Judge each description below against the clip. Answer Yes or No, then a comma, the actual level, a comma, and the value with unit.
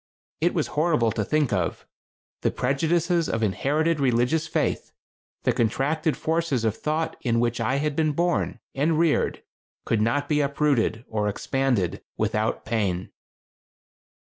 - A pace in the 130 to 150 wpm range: Yes, average, 140 wpm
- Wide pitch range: Yes, wide, 5.7 semitones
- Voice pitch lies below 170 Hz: Yes, medium, 140 Hz